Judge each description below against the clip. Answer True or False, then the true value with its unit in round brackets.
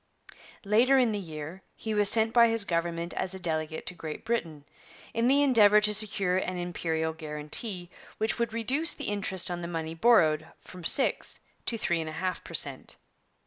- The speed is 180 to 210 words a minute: True (185 wpm)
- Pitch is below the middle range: False (185 Hz)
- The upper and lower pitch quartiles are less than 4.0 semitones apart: False (5.3 semitones)